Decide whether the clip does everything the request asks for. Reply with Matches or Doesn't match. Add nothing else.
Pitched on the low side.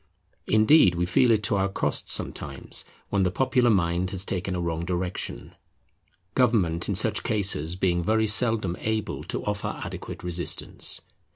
Matches